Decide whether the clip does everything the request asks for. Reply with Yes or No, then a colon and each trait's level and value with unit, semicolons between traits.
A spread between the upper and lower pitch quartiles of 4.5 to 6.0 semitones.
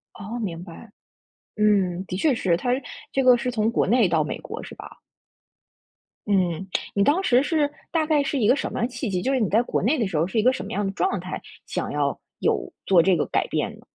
Yes: average, 5.2 semitones